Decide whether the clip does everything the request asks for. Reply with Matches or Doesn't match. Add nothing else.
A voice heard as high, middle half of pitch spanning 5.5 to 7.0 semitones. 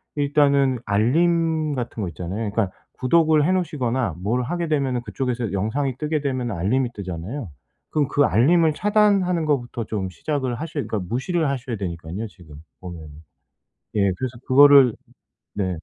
Doesn't match